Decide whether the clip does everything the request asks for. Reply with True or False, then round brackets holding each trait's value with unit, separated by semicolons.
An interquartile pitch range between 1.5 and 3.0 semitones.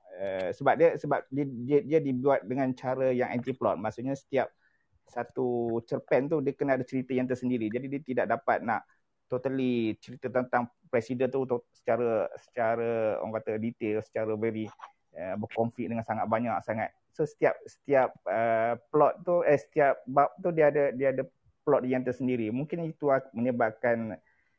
True (2.7 semitones)